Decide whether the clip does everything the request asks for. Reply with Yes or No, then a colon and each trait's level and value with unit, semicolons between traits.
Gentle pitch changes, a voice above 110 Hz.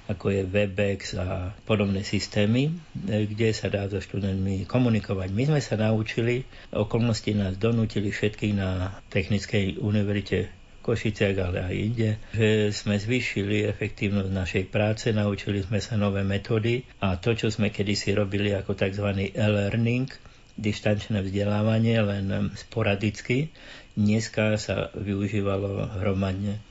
No: narrow, 1.8 semitones; low, 105 Hz